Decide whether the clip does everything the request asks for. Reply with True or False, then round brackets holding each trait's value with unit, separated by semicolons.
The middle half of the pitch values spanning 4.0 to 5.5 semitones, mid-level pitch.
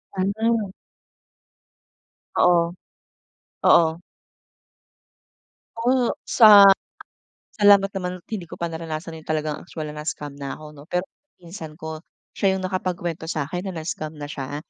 False (3.6 semitones; 170 Hz)